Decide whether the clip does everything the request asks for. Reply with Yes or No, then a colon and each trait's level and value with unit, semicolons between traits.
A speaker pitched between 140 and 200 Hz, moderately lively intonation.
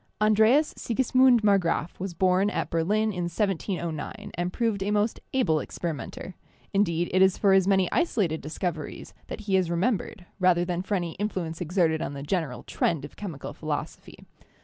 Yes: medium, 185 Hz; average, 3.8 semitones